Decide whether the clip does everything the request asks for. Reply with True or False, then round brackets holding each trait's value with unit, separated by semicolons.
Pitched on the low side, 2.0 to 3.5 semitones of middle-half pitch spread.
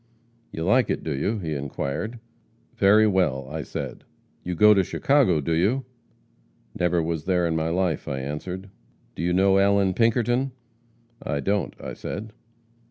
False (95 Hz; 4.7 semitones)